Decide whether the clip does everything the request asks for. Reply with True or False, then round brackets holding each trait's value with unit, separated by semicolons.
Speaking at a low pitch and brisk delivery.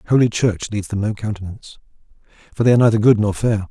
True (110 Hz; 210 wpm)